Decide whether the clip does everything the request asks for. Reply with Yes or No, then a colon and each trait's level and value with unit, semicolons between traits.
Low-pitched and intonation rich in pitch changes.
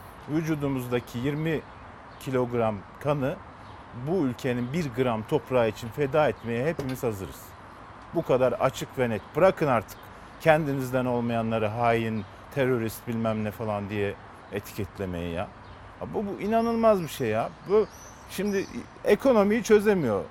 Yes: low, 125 Hz; wide, 5.7 semitones